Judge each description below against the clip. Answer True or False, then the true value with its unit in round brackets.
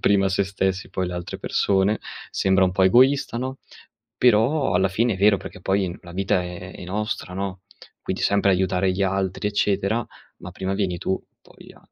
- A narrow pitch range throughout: True (1.8 semitones)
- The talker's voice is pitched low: True (95 Hz)